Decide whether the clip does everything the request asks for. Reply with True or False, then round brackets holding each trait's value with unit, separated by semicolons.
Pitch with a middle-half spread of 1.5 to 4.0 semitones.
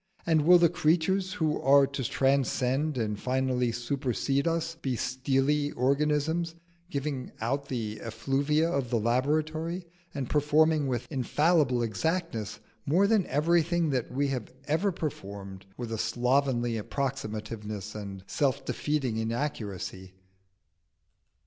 False (4.5 semitones)